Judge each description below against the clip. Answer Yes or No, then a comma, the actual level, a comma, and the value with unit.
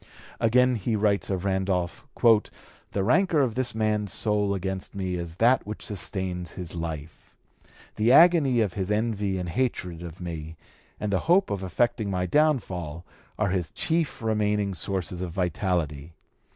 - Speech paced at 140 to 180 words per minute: Yes, average, 150 wpm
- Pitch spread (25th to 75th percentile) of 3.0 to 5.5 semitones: Yes, average, 3.9 semitones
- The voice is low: Yes, low, 100 Hz